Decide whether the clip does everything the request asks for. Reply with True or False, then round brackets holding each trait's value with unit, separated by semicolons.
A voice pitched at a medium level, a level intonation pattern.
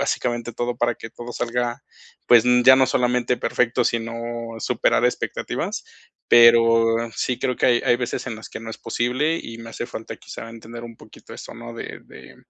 False (120 Hz; 1.1 semitones)